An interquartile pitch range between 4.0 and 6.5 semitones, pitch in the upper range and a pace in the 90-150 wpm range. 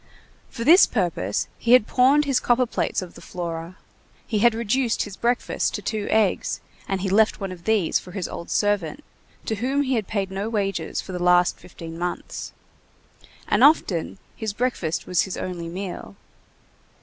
No: average, 4.8 semitones; high, 200 Hz; average, 175 wpm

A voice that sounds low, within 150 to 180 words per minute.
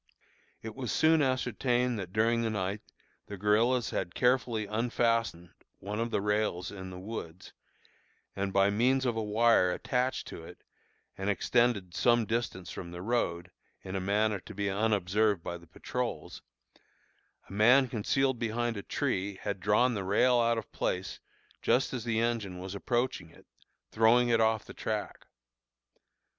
Yes: low, 110 Hz; average, 160 wpm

